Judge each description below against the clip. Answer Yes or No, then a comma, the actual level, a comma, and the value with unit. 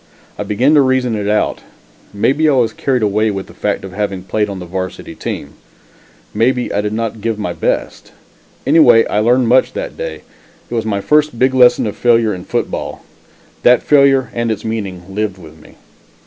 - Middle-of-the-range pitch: No, low, 110 Hz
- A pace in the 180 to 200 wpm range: Yes, average, 190 wpm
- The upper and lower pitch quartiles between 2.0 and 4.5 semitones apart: Yes, average, 4.1 semitones